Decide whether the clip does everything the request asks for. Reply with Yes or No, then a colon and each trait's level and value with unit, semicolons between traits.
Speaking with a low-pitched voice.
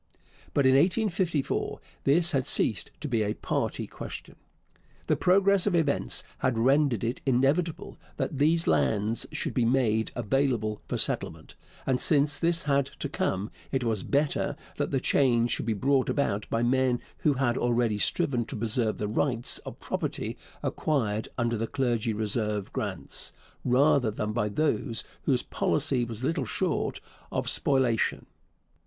Yes: low, 125 Hz